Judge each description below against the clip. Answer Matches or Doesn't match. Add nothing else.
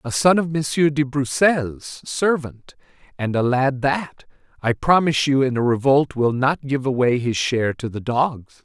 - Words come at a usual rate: Matches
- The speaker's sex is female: Doesn't match